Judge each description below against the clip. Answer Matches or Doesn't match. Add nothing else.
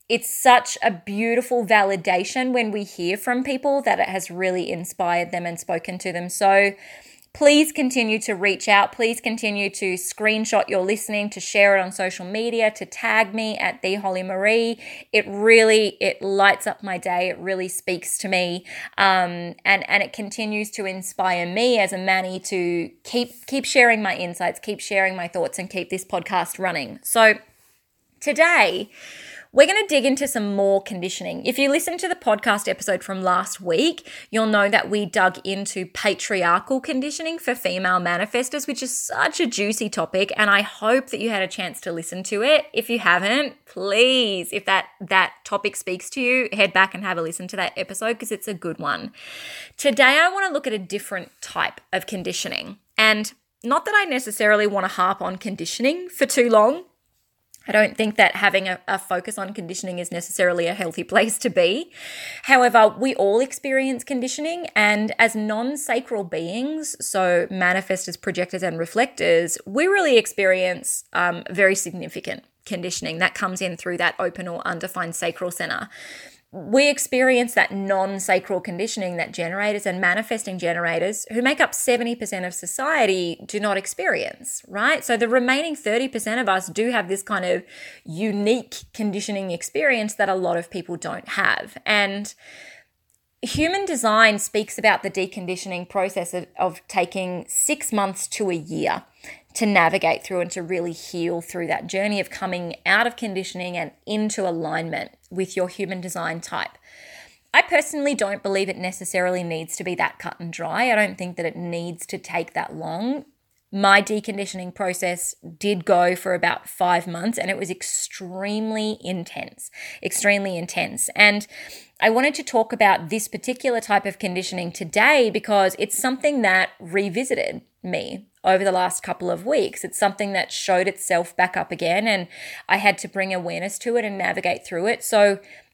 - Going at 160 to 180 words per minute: Matches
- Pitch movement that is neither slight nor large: Matches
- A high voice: Matches